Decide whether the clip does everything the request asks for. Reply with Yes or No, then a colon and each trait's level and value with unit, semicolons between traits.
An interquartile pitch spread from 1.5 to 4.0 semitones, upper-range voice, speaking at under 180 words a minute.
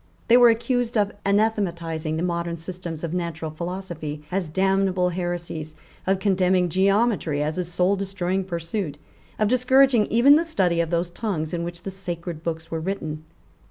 No: average, 3.0 semitones; medium, 180 Hz; average, 160 wpm